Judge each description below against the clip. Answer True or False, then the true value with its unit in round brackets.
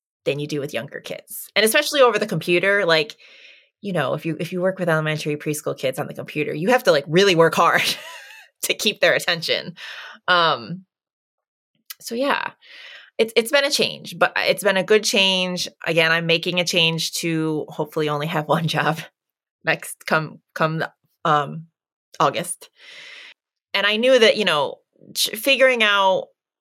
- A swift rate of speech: False (170 wpm)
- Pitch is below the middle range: False (180 Hz)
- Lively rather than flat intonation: True (6.0 semitones)